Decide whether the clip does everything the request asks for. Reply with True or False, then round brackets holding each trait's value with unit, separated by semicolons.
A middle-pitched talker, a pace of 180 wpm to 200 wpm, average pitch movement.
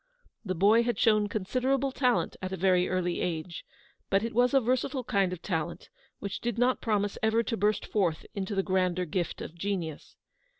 False (200 Hz; 185 wpm; 4.3 semitones)